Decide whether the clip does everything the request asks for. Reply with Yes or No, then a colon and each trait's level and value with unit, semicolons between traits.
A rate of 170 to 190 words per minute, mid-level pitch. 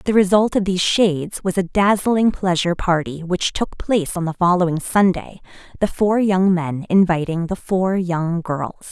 Yes: average, 175 wpm; medium, 180 Hz